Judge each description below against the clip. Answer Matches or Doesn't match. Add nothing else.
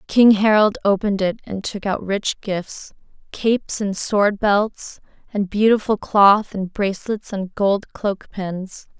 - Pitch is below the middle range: Doesn't match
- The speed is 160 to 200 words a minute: Doesn't match